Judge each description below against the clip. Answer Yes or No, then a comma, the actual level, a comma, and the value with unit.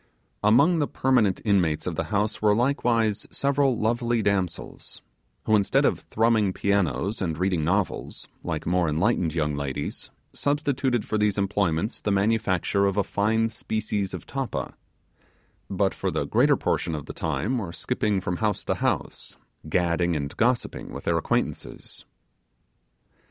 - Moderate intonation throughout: Yes, average, 4.1 semitones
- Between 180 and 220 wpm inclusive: No, average, 145 wpm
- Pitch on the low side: Yes, low, 100 Hz